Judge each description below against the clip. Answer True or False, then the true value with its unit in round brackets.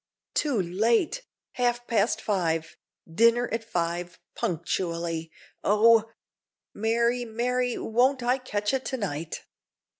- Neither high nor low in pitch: False (225 Hz)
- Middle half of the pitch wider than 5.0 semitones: True (5.5 semitones)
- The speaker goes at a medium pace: False (110 wpm)